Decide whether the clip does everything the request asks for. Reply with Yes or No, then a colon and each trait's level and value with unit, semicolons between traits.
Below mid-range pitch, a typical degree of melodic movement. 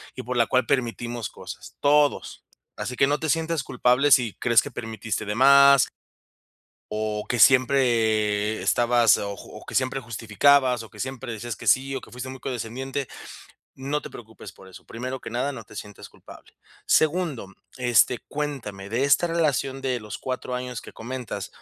Yes: low, 125 Hz; average, 3.3 semitones